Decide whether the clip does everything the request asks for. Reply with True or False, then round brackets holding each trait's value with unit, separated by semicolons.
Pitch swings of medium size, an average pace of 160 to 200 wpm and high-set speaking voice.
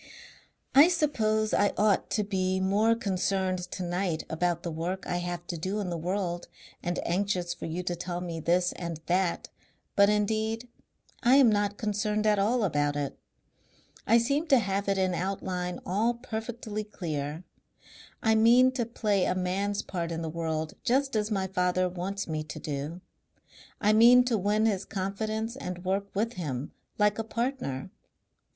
True (3.7 semitones; 170 wpm; 195 Hz)